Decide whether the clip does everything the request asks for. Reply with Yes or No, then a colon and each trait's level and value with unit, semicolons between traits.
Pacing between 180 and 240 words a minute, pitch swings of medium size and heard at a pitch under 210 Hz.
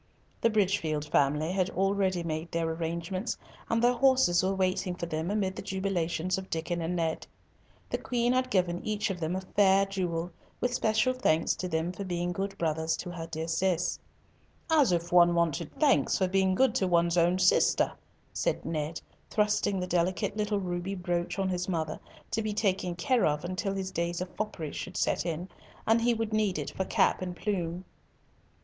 Yes: average, 190 wpm; average, 3.0 semitones; medium, 185 Hz